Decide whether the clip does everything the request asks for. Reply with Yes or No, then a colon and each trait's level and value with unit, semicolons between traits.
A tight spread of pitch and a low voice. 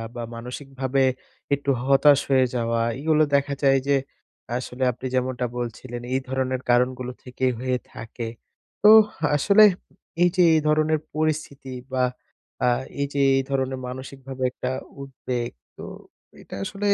Yes: narrow, 2.0 semitones; low, 130 Hz